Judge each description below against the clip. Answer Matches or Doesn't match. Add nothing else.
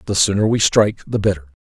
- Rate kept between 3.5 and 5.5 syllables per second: Doesn't match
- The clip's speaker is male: Matches